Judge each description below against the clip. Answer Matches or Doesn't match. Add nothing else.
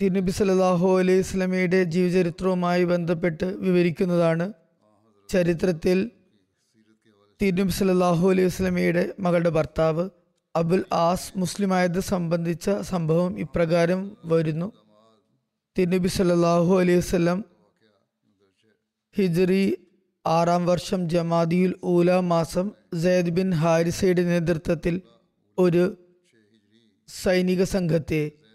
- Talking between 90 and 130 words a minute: Doesn't match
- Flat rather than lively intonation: Matches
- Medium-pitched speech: Matches